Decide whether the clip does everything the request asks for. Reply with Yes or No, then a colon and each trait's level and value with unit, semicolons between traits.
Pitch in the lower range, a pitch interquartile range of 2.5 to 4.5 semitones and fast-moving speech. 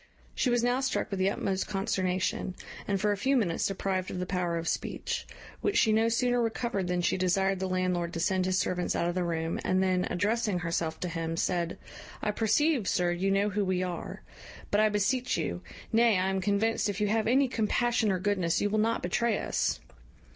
No: high, 195 Hz; average, 3.4 semitones; fast, 210 wpm